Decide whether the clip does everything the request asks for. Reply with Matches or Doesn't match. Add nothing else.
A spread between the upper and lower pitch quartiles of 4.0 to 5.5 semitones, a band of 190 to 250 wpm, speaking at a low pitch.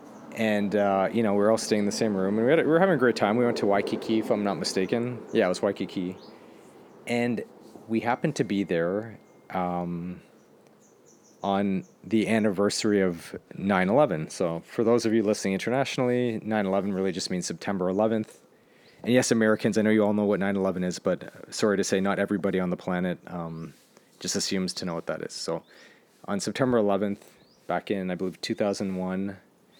Doesn't match